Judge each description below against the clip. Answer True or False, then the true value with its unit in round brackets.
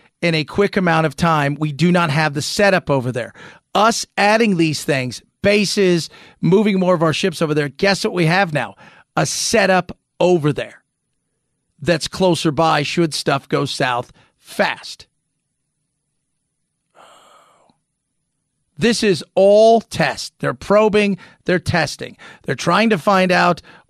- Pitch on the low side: False (170 Hz)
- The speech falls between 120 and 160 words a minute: True (140 wpm)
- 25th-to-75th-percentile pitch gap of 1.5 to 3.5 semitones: False (4.6 semitones)